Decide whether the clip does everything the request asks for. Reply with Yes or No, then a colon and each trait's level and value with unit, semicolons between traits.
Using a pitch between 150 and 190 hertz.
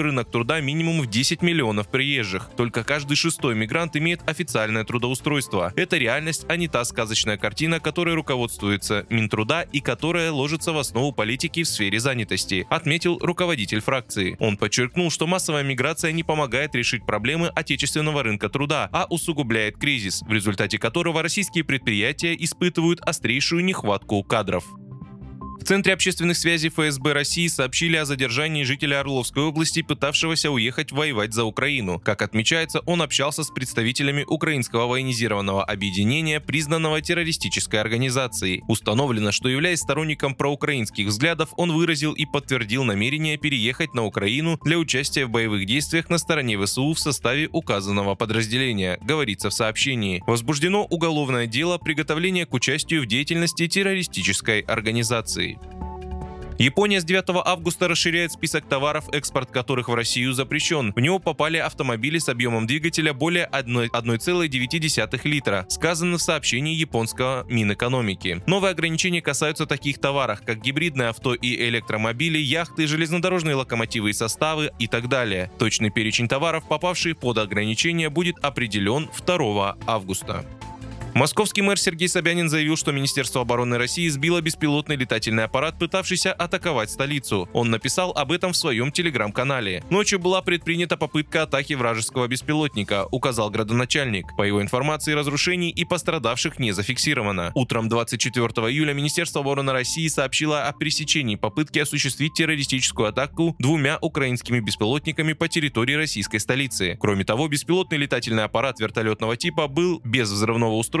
No: medium, 140 Hz